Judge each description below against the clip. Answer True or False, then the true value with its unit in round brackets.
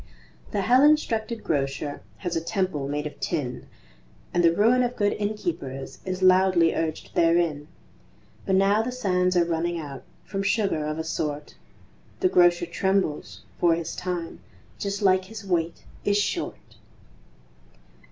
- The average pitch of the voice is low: False (180 Hz)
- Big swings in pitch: False (3.7 semitones)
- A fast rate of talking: False (145 wpm)